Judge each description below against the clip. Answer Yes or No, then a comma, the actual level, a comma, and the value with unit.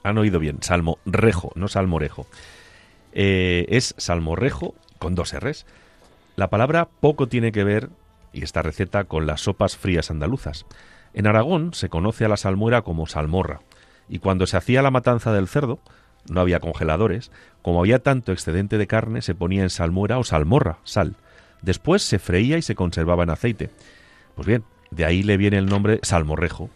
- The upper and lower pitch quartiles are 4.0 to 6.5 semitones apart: Yes, average, 4.3 semitones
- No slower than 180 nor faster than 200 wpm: No, average, 170 wpm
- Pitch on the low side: Yes, very low, 95 Hz